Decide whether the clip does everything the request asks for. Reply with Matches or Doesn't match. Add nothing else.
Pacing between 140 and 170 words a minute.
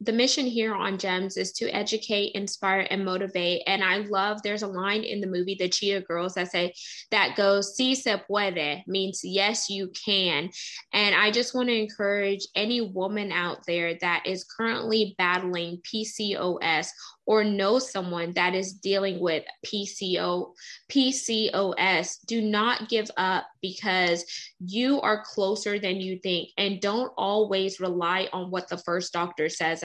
Matches